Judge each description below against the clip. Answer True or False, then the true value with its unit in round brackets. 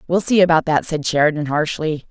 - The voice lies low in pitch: False (160 Hz)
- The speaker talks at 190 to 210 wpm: True (200 wpm)